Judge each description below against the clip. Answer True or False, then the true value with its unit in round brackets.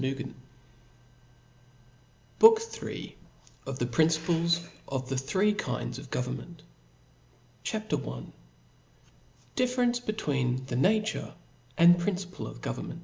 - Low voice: False (165 Hz)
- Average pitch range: False (7.7 semitones)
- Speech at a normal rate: False (100 wpm)